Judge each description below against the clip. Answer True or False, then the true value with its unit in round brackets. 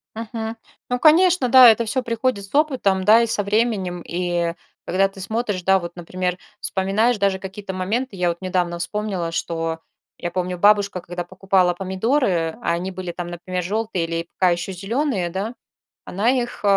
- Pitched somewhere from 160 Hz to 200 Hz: True (190 Hz)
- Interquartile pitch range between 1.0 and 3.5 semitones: False (4.0 semitones)